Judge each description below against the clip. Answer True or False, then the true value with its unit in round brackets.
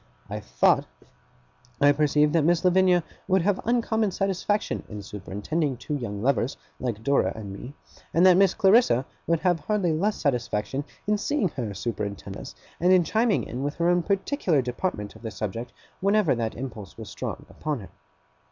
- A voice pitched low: False (150 Hz)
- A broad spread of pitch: True (8.2 semitones)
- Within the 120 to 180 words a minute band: True (170 wpm)